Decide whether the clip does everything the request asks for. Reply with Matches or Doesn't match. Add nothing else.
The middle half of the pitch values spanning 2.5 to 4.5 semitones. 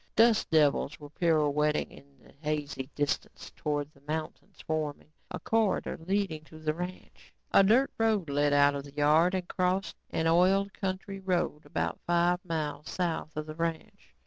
Matches